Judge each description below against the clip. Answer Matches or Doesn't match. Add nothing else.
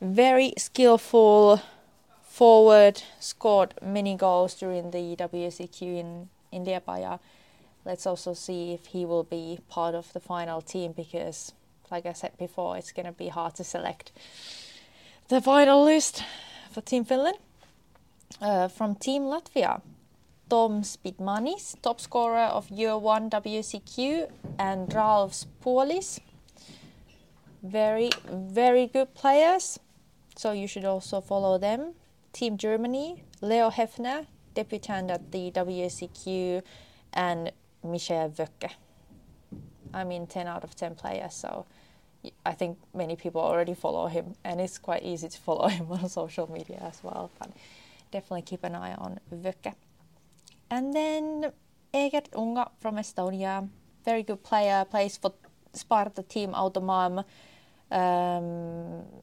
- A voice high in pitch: Matches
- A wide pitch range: Doesn't match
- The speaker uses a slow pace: Matches